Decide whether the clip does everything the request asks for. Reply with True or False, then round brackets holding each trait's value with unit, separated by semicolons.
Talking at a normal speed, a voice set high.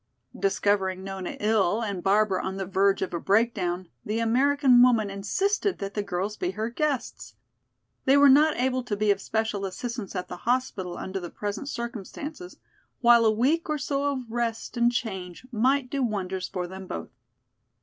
True (175 wpm; 220 Hz)